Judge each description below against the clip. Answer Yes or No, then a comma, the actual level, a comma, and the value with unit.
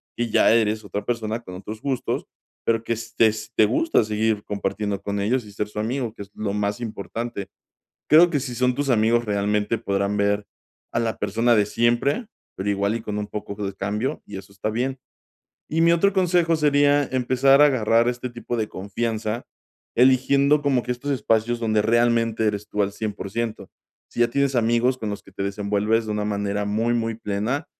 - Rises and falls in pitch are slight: No, average, 3.1 semitones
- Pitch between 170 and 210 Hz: No, low, 115 Hz